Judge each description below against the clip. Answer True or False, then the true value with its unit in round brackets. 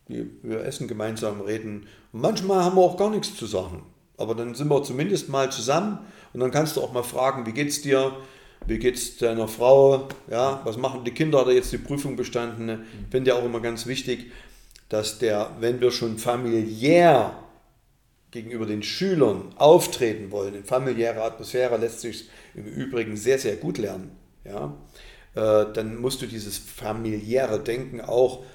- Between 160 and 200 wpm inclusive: True (170 wpm)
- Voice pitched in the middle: False (120 Hz)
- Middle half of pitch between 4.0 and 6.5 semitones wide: False (3.1 semitones)